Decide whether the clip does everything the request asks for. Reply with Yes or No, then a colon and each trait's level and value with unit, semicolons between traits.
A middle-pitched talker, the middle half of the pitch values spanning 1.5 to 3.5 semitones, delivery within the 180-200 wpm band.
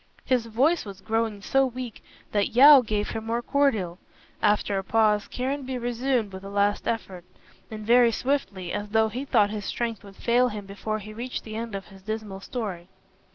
No: high, 220 Hz; average, 3.2 semitones; average, 190 wpm